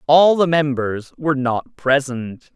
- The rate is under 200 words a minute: Yes, average, 140 wpm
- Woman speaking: No, male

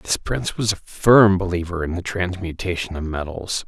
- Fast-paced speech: No, average, 180 wpm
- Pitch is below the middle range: Yes, very low, 90 Hz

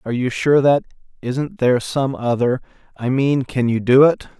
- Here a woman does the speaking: No, male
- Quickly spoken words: No, average, 165 wpm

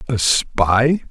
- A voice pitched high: No, low, 125 Hz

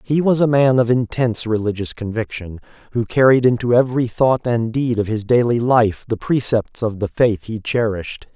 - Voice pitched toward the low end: Yes, low, 115 Hz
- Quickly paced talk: No, average, 185 wpm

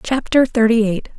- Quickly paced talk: No, average, 150 wpm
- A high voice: Yes, high, 230 Hz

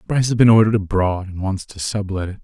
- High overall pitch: No, low, 100 Hz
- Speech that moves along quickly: Yes, fast, 245 wpm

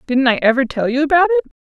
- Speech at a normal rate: No, fast, 255 wpm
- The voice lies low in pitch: No, very high, 280 Hz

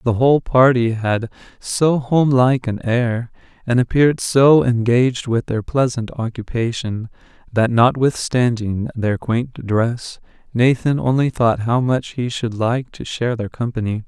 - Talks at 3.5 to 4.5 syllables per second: Yes, 4.2 syllables/s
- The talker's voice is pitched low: Yes, low, 120 Hz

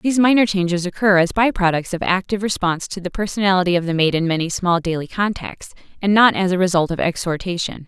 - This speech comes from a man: No, female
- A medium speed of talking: No, fast, 215 wpm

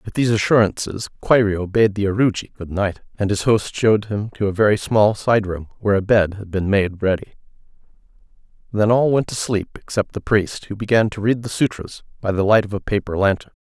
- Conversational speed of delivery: No, fast, 210 wpm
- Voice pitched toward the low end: Yes, low, 105 Hz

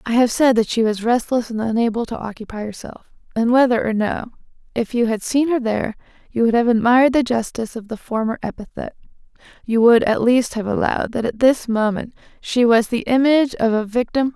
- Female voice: Yes, female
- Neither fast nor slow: No, fast, 215 wpm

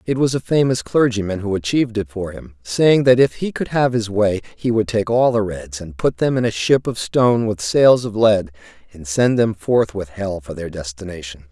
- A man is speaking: Yes, male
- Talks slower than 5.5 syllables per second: Yes, 5.0 syllables/s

